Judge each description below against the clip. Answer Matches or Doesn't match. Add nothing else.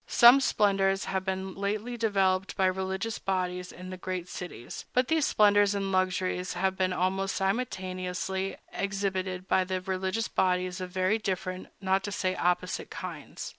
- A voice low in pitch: Doesn't match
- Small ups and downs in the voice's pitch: Matches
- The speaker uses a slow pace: Doesn't match